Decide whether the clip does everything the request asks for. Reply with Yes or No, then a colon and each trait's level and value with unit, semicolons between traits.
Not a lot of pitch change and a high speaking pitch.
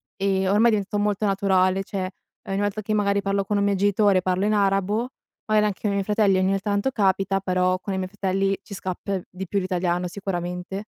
Yes: narrow, 1.5 semitones; high, 195 Hz